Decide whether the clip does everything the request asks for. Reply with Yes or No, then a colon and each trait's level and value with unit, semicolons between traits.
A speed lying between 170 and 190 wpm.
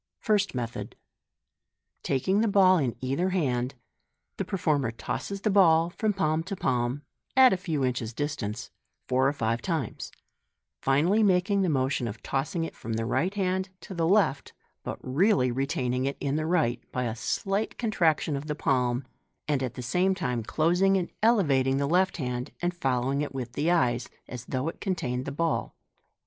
Yes: average, 180 wpm